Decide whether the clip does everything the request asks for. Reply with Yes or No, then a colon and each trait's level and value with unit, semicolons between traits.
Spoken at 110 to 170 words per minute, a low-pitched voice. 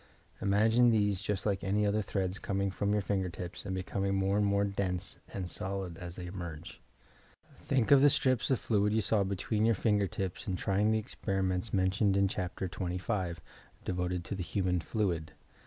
No: average, 185 wpm; low, 100 Hz